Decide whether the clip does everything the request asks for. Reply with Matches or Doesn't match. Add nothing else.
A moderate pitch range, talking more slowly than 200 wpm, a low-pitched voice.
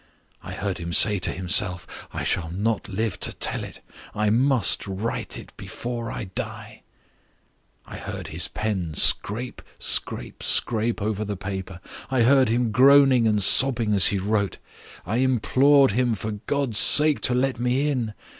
Matches